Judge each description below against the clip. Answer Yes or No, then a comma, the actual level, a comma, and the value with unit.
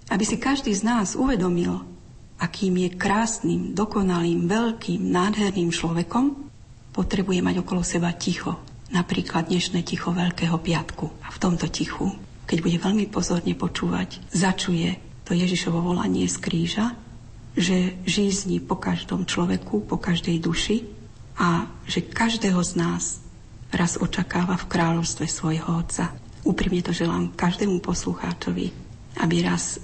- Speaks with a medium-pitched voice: Yes, medium, 175 Hz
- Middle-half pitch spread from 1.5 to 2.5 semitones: No, average, 2.9 semitones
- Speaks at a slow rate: No, average, 130 wpm